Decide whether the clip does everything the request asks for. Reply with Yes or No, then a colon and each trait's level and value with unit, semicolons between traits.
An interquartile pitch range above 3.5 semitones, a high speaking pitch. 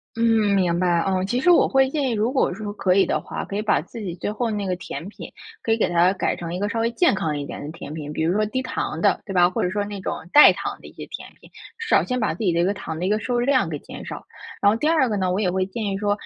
Yes: average, 4.1 semitones; high, 205 Hz